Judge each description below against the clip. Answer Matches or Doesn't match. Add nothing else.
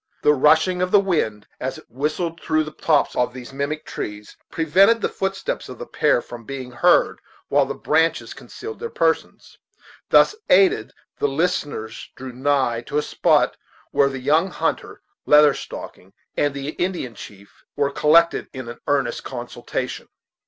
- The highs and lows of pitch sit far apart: Doesn't match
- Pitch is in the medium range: Matches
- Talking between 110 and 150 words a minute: Doesn't match